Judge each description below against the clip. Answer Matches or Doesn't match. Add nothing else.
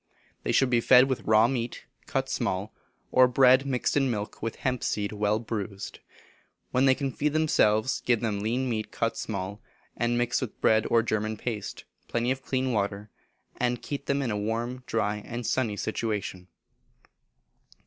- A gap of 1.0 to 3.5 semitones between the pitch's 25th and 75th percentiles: Matches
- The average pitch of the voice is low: Matches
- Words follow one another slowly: Doesn't match